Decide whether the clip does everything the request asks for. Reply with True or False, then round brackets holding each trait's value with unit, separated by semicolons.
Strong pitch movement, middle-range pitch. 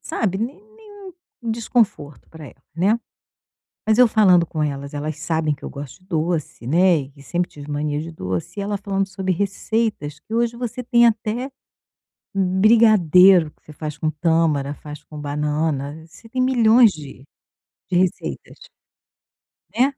True (6.7 semitones; 180 Hz)